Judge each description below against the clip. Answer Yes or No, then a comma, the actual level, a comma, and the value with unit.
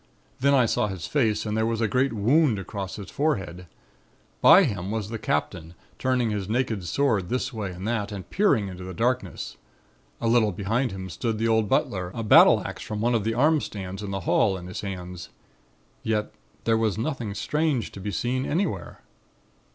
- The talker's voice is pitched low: Yes, low, 110 Hz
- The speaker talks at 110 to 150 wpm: No, average, 195 wpm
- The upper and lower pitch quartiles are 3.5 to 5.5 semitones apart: Yes, average, 3.9 semitones